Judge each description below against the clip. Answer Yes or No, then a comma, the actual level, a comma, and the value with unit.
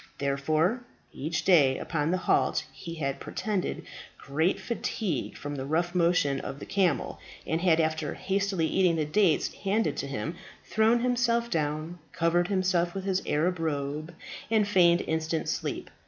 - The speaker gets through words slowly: No, average, 155 wpm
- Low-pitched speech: No, medium, 170 Hz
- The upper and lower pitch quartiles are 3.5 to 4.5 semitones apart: Yes, average, 3.8 semitones